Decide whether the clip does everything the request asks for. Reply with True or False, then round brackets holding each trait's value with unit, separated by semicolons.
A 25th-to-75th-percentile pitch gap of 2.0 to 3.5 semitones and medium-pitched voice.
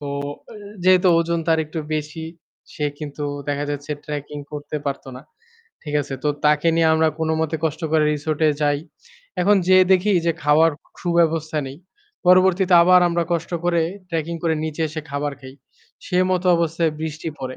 True (2.4 semitones; 160 Hz)